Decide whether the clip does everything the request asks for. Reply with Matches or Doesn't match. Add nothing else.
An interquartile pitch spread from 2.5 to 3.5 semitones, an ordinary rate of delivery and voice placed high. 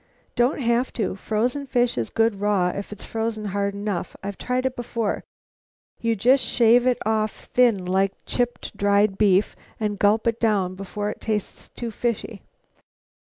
Matches